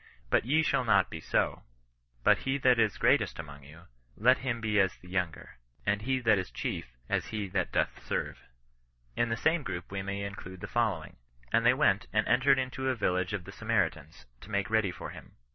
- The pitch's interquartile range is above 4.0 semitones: Yes, average, 4.6 semitones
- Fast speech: Yes, fast, 210 wpm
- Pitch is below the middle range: Yes, low, 105 Hz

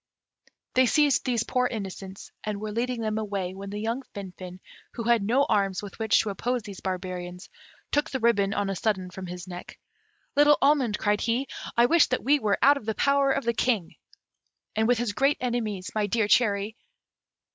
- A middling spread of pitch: Yes, average, 4.1 semitones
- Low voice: No, high, 220 Hz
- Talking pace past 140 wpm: Yes, average, 195 wpm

